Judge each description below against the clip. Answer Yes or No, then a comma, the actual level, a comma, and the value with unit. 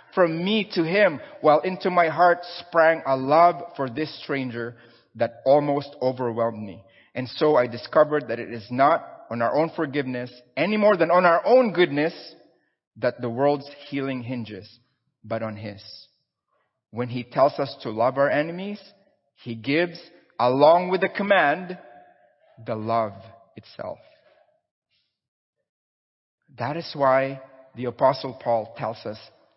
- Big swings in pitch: Yes, wide, 6.2 semitones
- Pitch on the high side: No, medium, 140 Hz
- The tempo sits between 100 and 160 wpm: Yes, average, 140 wpm